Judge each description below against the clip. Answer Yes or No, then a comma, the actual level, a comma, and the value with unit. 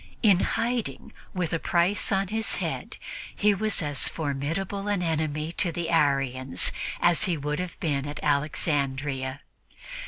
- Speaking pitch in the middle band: Yes, medium, 160 Hz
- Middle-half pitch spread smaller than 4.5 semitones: No, average, 4.8 semitones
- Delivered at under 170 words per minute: Yes, average, 145 wpm